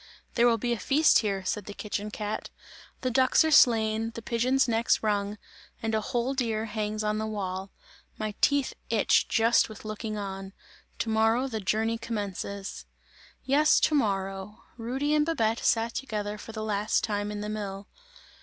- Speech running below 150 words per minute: No, average, 175 wpm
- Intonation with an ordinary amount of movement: No, narrow, 2.2 semitones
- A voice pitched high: Yes, high, 220 Hz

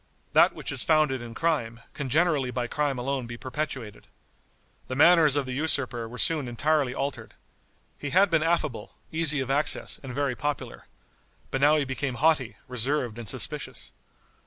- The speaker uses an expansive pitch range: No, average, 3.7 semitones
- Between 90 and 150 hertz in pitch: Yes, medium, 140 Hz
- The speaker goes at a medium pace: Yes, average, 165 wpm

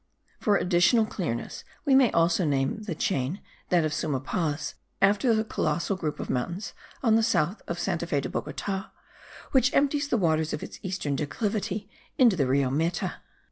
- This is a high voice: No, medium, 180 Hz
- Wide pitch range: Yes, wide, 6.1 semitones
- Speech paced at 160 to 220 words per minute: Yes, average, 175 wpm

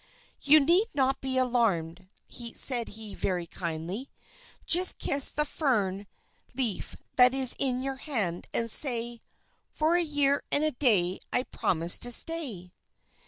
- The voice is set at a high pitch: Yes, very high, 250 Hz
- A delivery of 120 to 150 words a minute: Yes, average, 140 wpm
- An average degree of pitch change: No, wide, 6.1 semitones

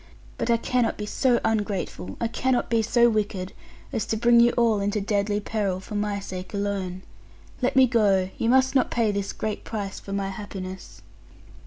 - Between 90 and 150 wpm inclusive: No, average, 185 wpm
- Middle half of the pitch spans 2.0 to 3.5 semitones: Yes, average, 2.9 semitones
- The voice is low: No, high, 210 Hz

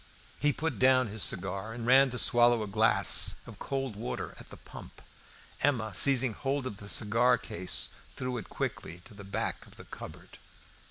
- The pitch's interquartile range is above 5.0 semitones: No, average, 4.3 semitones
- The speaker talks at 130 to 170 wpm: No, average, 180 wpm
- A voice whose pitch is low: Yes, low, 120 Hz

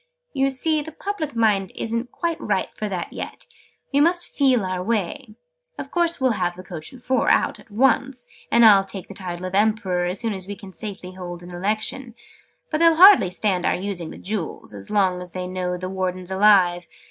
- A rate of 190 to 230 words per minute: Yes, fast, 205 wpm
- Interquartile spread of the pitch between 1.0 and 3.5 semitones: No, wide, 5.5 semitones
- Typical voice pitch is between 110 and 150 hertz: No, high, 200 Hz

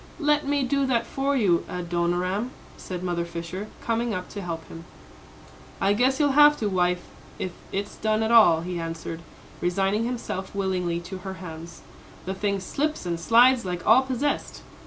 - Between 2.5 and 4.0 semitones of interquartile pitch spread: No, wide, 5.4 semitones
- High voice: Yes, high, 195 Hz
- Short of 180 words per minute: Yes, average, 170 wpm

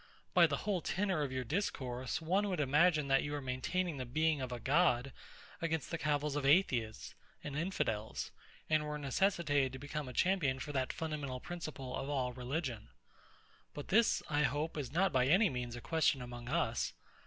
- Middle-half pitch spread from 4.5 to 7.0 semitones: No, average, 4.1 semitones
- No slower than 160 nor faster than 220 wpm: Yes, average, 185 wpm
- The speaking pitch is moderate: Yes, medium, 145 Hz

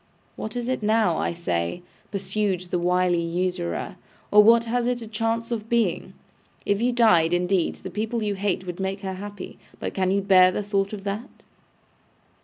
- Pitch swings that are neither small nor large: Yes, average, 3.4 semitones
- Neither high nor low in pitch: No, high, 200 Hz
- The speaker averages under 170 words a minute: No, average, 185 wpm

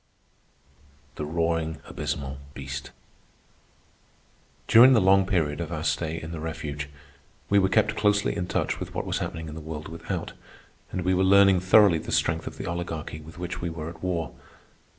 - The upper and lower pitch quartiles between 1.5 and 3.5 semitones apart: Yes, average, 3.2 semitones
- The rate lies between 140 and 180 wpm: Yes, average, 175 wpm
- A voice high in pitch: No, very low, 85 Hz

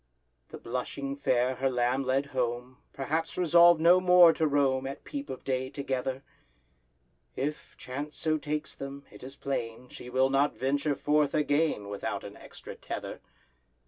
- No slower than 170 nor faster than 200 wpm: No, average, 155 wpm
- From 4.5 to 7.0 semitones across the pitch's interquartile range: No, average, 2.7 semitones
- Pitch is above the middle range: No, medium, 140 Hz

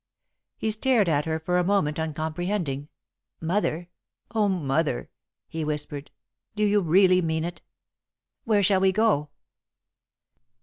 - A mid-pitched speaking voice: Yes, medium, 175 Hz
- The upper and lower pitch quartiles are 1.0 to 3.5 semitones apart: No, average, 4.5 semitones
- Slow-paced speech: Yes, slow, 125 wpm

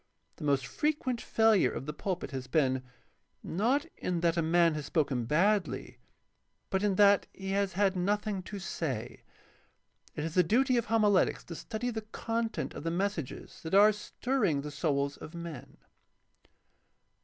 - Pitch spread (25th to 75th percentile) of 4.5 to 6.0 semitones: Yes, wide, 5.6 semitones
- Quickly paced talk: No, average, 165 wpm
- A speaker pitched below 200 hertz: Yes, medium, 185 Hz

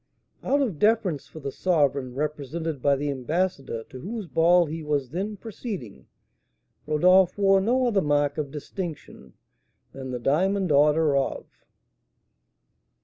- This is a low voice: No, medium, 155 Hz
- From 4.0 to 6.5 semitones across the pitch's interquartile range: Yes, average, 5.3 semitones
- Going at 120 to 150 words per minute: Yes, slow, 135 wpm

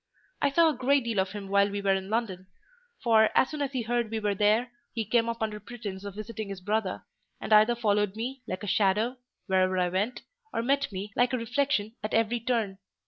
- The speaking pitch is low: No, high, 220 Hz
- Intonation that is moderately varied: Yes, average, 3.2 semitones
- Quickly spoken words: Yes, fast, 225 wpm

